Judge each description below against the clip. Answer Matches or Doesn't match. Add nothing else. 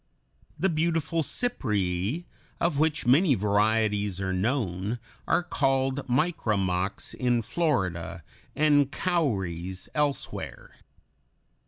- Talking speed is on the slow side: Matches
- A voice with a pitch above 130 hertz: Doesn't match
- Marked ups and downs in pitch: Matches